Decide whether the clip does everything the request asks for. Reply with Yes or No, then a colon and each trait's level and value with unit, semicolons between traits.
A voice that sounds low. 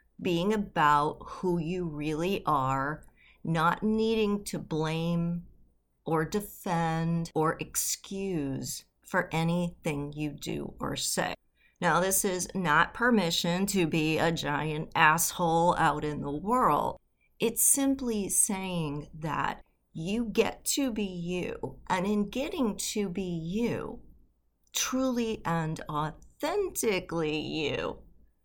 No: medium, 170 Hz